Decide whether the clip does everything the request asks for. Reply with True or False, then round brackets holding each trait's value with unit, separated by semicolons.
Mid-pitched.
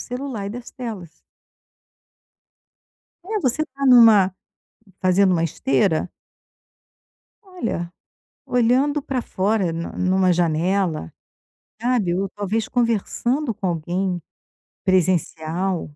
False (195 Hz)